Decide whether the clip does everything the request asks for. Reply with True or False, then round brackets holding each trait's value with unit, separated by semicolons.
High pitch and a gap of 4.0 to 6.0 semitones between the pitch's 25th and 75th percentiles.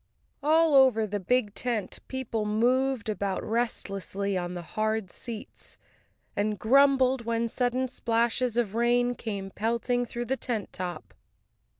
False (230 Hz; 3.2 semitones)